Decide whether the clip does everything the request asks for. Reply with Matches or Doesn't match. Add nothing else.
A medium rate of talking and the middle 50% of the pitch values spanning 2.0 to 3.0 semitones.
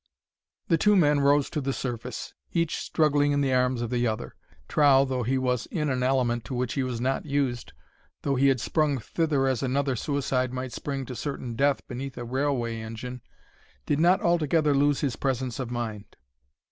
Matches